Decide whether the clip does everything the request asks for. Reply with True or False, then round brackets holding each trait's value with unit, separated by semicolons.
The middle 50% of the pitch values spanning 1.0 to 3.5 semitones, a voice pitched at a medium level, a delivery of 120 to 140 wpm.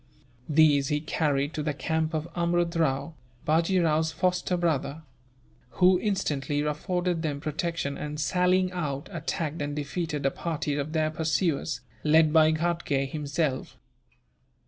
True (2.6 semitones; 155 Hz; 135 wpm)